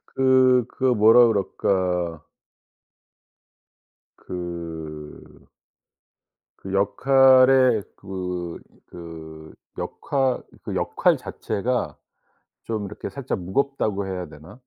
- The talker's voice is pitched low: Yes, low, 100 Hz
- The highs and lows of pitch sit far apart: Yes, wide, 6.7 semitones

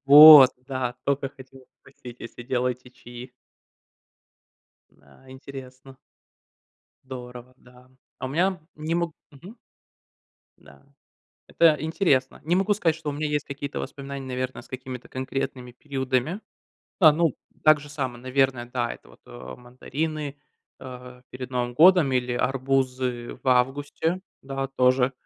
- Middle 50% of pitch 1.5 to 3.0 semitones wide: Yes, average, 2.7 semitones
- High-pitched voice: No, low, 130 Hz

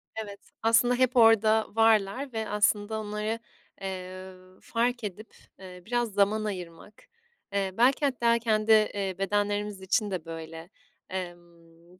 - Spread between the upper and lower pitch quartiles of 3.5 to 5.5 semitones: No, average, 3.1 semitones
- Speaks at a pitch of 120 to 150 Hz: No, high, 210 Hz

